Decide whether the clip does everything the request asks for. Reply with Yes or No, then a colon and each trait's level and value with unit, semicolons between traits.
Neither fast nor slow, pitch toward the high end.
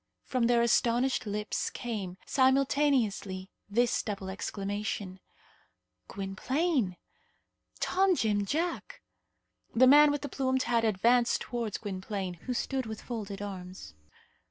No: slow, 110 wpm; high, 230 Hz